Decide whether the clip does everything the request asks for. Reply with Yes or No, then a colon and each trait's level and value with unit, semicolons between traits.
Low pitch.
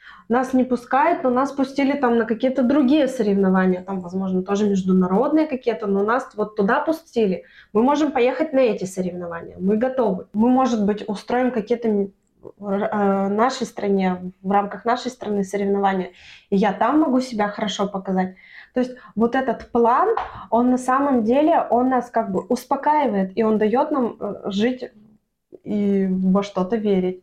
No: high, 220 Hz